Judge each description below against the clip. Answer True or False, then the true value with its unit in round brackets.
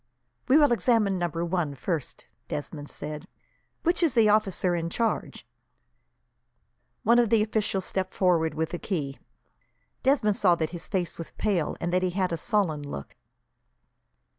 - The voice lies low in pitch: False (185 Hz)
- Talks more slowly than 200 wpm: True (155 wpm)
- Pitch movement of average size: True (4.5 semitones)